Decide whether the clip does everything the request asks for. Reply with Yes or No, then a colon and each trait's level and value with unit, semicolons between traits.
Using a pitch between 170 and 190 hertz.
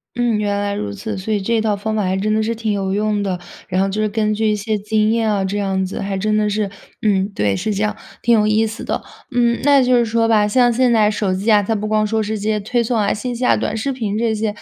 No: high, 215 Hz